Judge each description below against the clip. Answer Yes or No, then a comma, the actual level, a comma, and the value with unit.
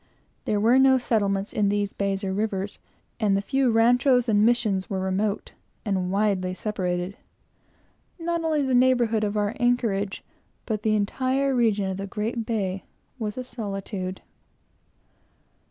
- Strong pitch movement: No, average, 3.5 semitones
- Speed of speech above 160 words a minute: No, average, 145 wpm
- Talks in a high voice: Yes, high, 210 Hz